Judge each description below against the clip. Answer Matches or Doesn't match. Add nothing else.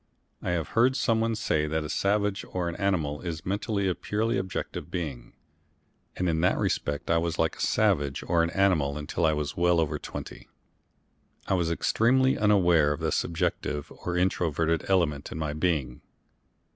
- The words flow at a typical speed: Matches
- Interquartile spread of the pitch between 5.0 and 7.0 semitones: Doesn't match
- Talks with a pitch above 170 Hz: Doesn't match